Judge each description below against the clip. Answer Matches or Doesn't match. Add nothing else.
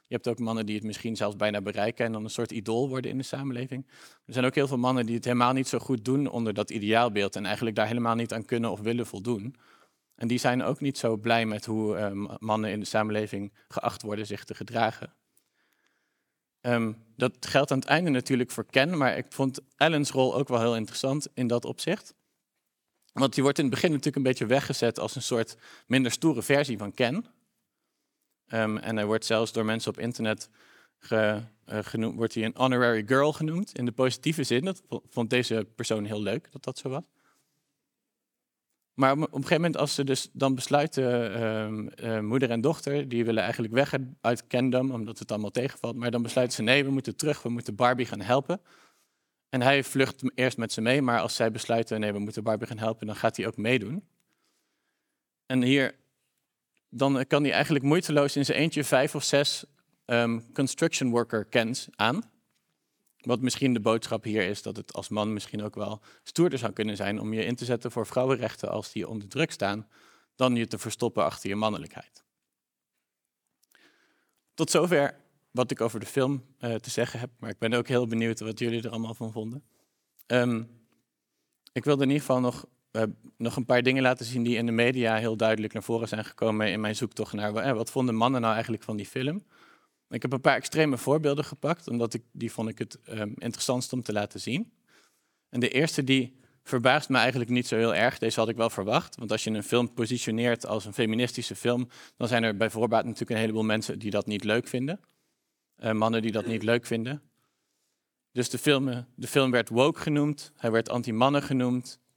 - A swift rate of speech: Matches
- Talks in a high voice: Doesn't match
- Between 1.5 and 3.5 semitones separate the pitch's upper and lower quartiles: Matches